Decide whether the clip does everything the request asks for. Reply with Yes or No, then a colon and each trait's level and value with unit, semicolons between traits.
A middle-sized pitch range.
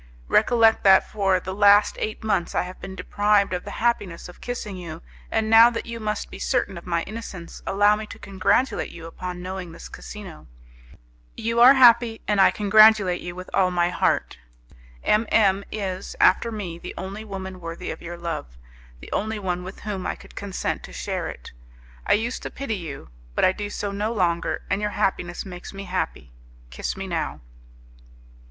Yes: average, 3.2 semitones